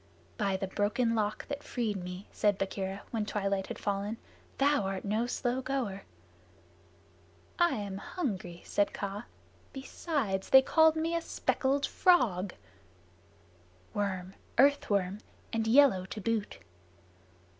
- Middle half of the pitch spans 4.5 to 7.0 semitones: Yes, average, 5.3 semitones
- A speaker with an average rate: No, slow, 125 wpm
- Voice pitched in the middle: No, high, 210 Hz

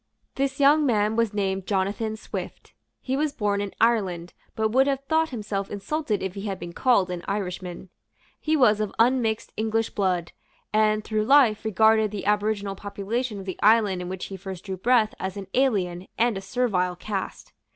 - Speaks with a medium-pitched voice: No, high, 210 Hz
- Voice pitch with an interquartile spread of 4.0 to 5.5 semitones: No, average, 3.2 semitones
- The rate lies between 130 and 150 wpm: No, average, 180 wpm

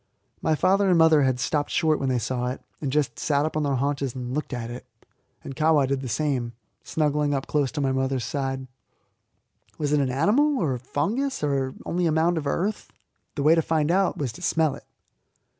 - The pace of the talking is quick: Yes, fast, 215 wpm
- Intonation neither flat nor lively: Yes, average, 3.3 semitones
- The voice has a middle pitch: Yes, medium, 145 Hz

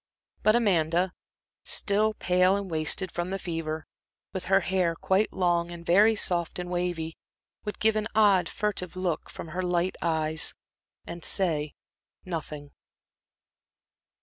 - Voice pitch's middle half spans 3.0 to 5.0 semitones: No, narrow, 2.6 semitones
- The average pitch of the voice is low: No, medium, 180 Hz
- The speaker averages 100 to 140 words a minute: Yes, slow, 135 wpm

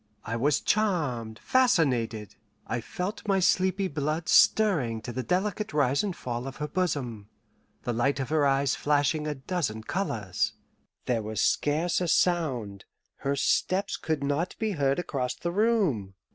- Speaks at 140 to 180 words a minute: Yes, average, 155 wpm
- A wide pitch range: Yes, wide, 6.8 semitones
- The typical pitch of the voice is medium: Yes, medium, 145 Hz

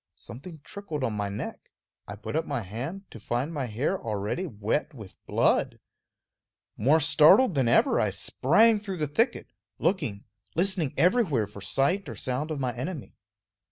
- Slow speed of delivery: No, average, 160 wpm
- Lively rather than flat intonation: Yes, wide, 7.5 semitones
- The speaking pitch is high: No, medium, 140 Hz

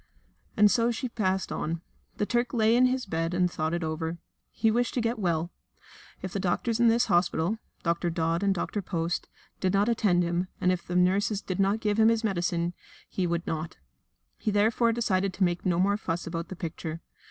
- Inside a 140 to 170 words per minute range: No, fast, 205 wpm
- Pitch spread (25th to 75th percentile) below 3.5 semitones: No, average, 4.2 semitones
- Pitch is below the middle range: No, medium, 185 Hz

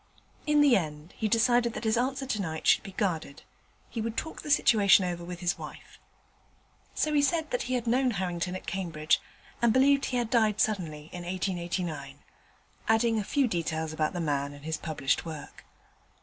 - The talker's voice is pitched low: No, high, 190 Hz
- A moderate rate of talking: Yes, average, 185 wpm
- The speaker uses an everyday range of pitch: No, wide, 6.9 semitones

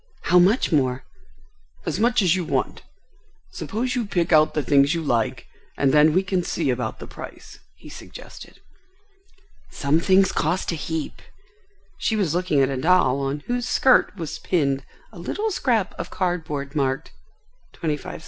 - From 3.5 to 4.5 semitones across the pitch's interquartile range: No, average, 5.0 semitones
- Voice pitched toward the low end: No, medium, 160 Hz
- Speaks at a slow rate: No, average, 165 wpm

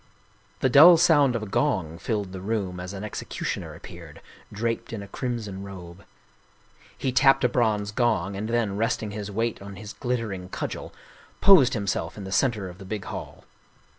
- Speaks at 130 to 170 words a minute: No, average, 180 wpm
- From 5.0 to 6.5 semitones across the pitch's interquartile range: No, average, 3.6 semitones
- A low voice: Yes, low, 105 Hz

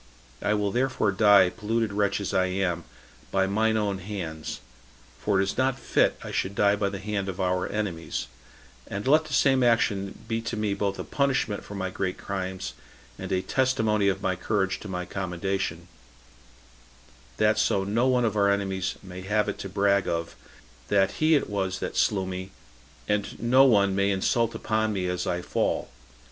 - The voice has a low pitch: Yes, low, 100 Hz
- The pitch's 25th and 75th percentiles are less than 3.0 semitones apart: Yes, narrow, 2.4 semitones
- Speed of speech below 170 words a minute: No, average, 185 wpm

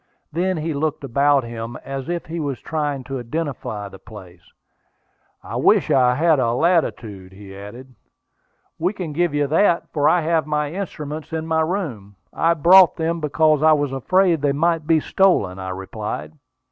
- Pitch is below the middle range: No, medium, 150 Hz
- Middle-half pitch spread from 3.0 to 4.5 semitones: No, average, 5.0 semitones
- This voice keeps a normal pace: Yes, average, 170 wpm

